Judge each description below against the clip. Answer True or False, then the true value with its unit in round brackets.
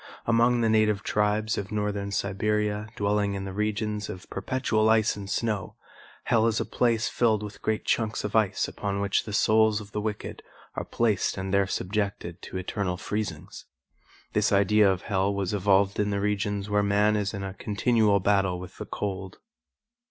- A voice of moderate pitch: False (105 Hz)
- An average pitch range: False (1.5 semitones)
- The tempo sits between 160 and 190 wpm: True (180 wpm)